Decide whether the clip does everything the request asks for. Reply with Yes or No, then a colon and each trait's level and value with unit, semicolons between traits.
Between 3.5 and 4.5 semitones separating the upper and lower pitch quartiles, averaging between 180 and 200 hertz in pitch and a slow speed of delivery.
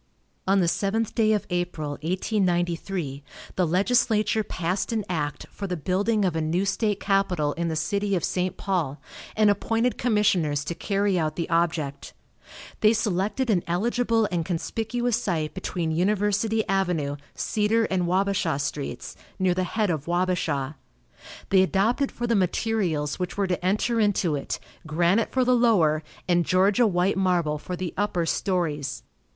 No: average, 3.8 semitones; medium, 185 Hz; average, 155 wpm